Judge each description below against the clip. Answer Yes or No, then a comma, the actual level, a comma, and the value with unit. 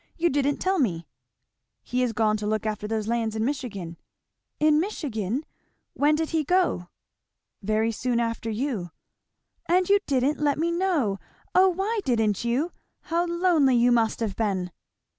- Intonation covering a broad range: Yes, wide, 6.8 semitones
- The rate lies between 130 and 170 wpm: Yes, average, 160 wpm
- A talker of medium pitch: No, very high, 250 Hz